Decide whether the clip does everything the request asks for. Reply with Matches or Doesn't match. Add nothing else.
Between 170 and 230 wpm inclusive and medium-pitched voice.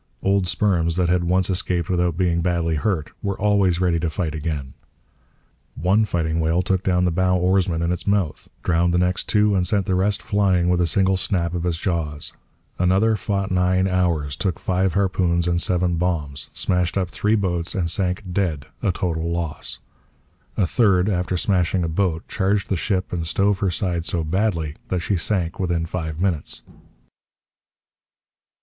Doesn't match